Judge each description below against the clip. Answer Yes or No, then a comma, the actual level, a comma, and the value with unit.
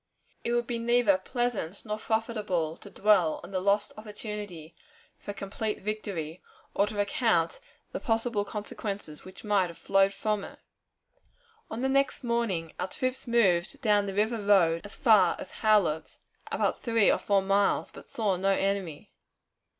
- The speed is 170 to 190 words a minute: No, average, 160 wpm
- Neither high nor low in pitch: No, high, 205 Hz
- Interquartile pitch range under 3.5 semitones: Yes, average, 2.9 semitones